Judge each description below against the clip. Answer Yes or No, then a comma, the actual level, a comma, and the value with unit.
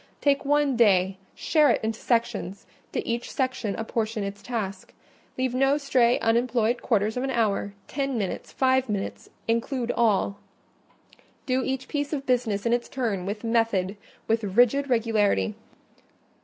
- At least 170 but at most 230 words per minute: No, average, 140 wpm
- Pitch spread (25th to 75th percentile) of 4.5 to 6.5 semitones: No, average, 3.7 semitones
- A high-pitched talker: Yes, high, 235 Hz